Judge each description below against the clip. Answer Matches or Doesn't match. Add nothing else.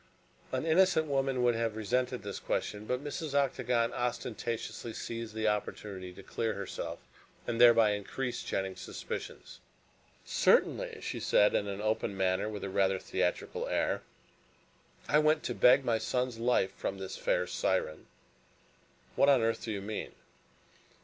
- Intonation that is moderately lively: Matches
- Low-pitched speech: Matches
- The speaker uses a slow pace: Doesn't match